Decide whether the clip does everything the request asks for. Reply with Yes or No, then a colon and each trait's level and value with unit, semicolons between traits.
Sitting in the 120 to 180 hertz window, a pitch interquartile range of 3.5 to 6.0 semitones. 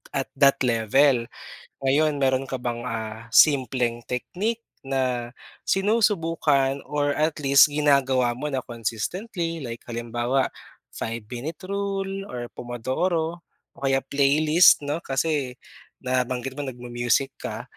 Yes: low, 135 Hz; average, 4.0 semitones